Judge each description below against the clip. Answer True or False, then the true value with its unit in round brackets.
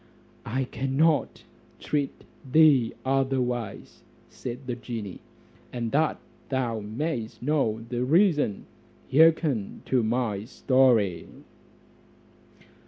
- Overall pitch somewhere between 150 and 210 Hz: False (130 Hz)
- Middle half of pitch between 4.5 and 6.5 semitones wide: False (3.5 semitones)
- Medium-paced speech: False (90 wpm)